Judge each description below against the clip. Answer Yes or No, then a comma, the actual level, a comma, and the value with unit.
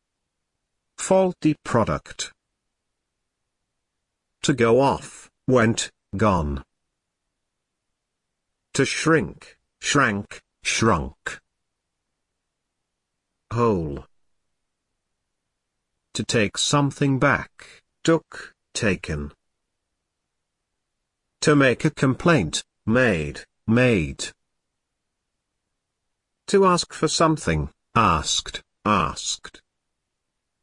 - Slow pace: Yes, slow, 60 wpm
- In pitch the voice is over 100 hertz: Yes, low, 120 Hz